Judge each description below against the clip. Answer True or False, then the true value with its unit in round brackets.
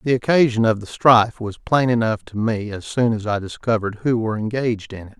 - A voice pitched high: False (110 Hz)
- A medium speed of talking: False (230 wpm)